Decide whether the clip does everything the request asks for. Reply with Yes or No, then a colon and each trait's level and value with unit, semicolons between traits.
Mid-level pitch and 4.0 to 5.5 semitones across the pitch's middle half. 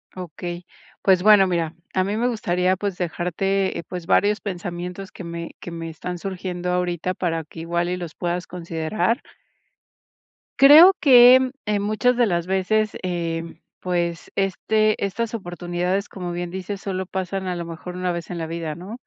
No: medium, 180 Hz; narrow, 2.4 semitones